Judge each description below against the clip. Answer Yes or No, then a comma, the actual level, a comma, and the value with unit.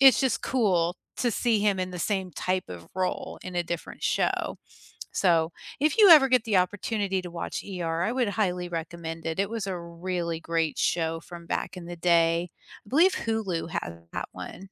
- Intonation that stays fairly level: No, average, 3.9 semitones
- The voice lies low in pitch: No, medium, 180 Hz